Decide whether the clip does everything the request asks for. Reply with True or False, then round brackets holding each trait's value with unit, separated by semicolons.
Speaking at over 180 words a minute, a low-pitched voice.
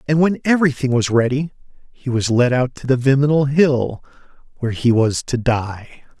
False (175 wpm; 130 Hz)